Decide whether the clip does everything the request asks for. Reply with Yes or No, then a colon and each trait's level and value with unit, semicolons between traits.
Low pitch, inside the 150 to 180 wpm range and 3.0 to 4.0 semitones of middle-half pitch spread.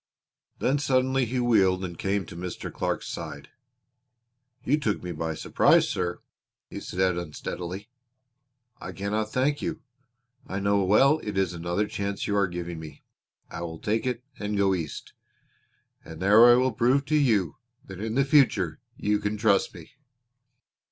No: low, 100 Hz; average, 160 wpm; wide, 5.4 semitones